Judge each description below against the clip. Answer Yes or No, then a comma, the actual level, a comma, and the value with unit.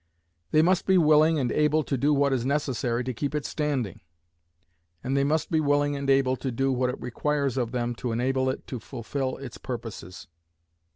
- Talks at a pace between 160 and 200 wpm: Yes, average, 195 wpm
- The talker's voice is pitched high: No, low, 135 Hz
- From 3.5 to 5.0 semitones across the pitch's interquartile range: No, average, 3.0 semitones